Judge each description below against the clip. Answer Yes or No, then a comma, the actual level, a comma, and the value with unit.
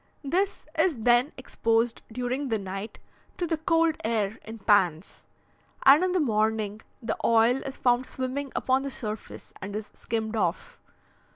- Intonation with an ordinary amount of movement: Yes, average, 4.1 semitones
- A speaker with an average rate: Yes, average, 155 wpm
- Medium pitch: No, high, 235 Hz